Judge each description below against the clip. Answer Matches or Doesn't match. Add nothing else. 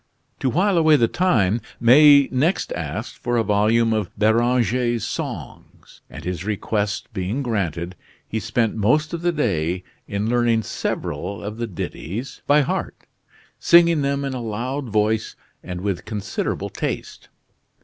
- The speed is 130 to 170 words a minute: Matches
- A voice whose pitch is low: Matches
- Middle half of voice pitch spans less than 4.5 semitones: Doesn't match